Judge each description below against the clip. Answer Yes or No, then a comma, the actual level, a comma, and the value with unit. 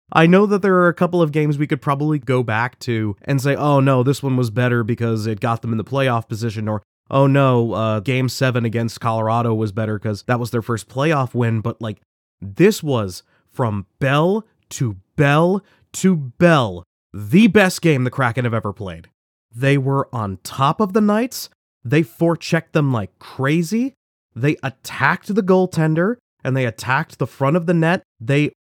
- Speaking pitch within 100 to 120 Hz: No, low, 130 Hz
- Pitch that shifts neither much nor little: No, wide, 5.8 semitones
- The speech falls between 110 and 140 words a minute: No, average, 190 wpm